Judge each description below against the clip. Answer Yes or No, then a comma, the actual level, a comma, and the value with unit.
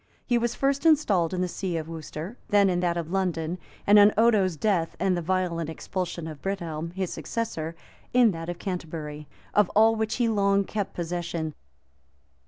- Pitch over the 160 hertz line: Yes, medium, 185 Hz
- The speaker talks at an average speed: Yes, average, 180 wpm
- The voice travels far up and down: No, average, 3.9 semitones